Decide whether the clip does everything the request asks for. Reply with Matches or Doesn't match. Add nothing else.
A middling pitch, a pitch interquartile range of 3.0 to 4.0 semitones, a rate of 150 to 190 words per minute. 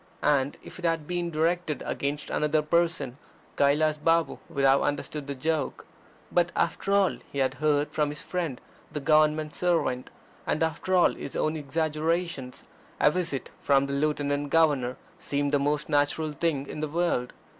Doesn't match